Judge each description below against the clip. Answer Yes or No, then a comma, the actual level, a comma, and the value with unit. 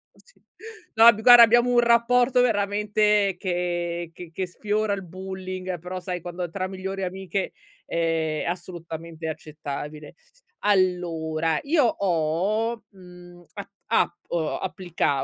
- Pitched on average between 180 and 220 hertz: Yes, medium, 185 Hz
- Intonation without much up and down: No, average, 3.4 semitones